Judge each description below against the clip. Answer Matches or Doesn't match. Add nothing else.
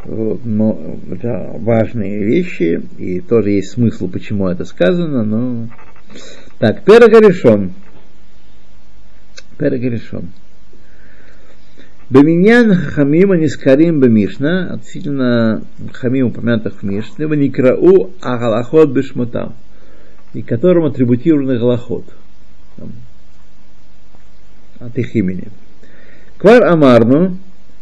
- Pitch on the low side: Matches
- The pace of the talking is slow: Matches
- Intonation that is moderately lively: Doesn't match